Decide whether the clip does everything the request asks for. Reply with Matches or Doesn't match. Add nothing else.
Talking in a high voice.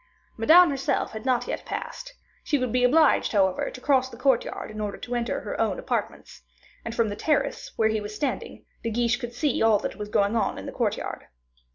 Matches